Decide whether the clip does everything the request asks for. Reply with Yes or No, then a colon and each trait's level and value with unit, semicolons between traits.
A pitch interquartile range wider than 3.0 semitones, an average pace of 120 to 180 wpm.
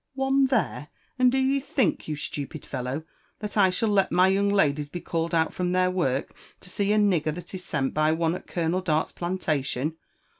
No: average, 4.6 semitones; average, 200 wpm